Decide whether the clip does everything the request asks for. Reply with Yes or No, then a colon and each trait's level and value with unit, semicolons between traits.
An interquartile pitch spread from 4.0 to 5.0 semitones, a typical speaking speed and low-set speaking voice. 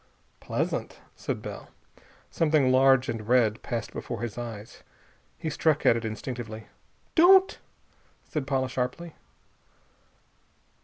No: average, 4.6 semitones; slow, 110 wpm; low, 130 Hz